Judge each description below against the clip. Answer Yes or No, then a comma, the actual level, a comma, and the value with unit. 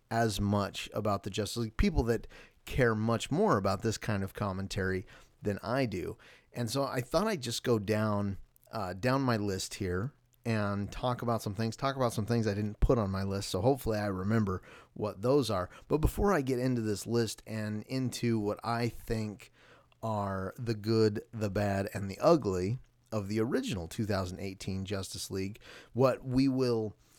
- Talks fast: No, average, 185 wpm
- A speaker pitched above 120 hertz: No, low, 110 Hz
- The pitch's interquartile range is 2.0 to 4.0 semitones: Yes, average, 3.1 semitones